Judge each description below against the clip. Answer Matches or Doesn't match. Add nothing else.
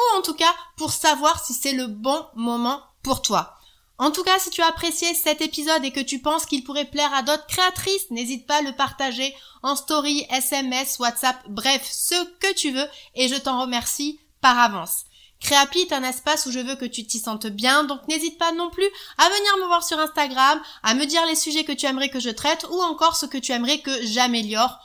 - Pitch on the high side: Matches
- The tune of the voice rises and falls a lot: Doesn't match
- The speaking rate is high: Matches